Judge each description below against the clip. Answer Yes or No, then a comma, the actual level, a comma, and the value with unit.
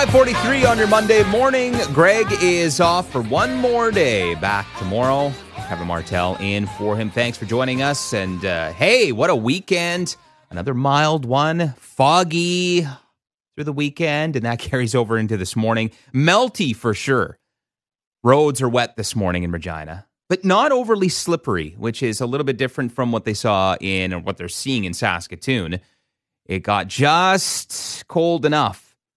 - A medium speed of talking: Yes, average, 165 wpm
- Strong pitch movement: Yes, wide, 8.4 semitones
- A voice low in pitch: Yes, low, 130 Hz